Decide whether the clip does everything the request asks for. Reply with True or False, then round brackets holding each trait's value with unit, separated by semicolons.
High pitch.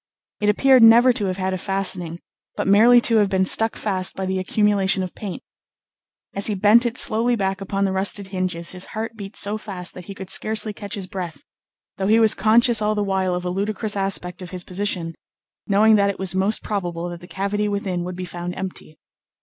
True (195 Hz)